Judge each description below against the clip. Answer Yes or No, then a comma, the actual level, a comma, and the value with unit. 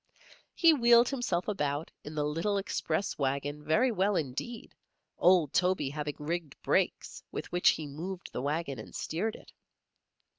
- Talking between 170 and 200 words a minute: No, average, 150 wpm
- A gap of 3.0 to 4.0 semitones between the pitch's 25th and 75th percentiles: No, average, 5.3 semitones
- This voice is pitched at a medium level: Yes, medium, 165 Hz